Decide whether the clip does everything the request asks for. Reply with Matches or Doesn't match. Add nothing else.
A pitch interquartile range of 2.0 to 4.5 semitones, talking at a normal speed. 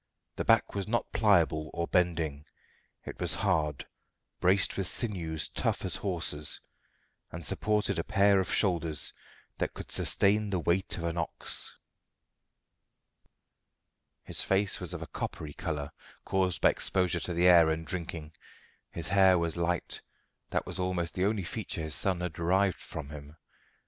Matches